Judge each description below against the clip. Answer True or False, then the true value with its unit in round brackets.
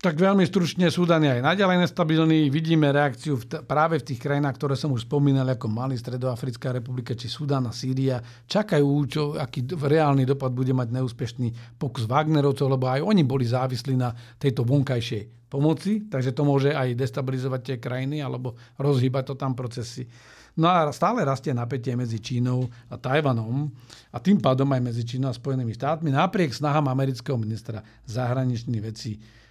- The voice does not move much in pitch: False (3.0 semitones)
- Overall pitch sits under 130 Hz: False (135 Hz)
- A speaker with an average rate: False (170 wpm)